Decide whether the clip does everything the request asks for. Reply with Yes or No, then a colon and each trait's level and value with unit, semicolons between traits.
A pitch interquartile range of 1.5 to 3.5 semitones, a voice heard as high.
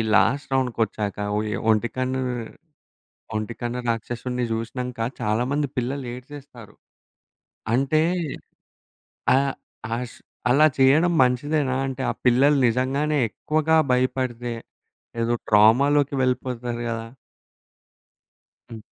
No: average, 2.7 semitones; low, 125 Hz